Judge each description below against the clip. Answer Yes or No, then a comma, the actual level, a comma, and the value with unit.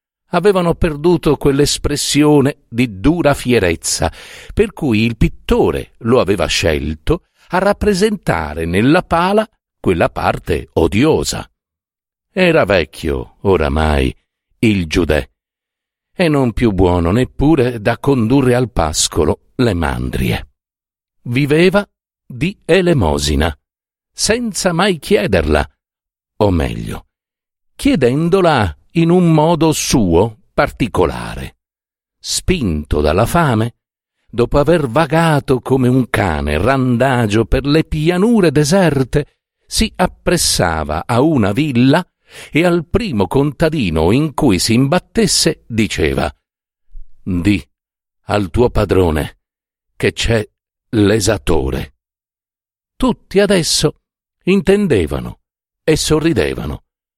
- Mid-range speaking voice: No, low, 125 Hz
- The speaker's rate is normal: No, slow, 95 wpm